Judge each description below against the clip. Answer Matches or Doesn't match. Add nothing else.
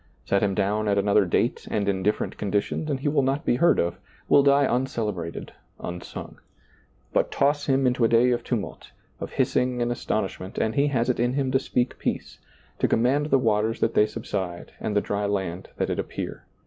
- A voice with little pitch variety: Doesn't match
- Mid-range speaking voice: Doesn't match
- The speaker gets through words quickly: Matches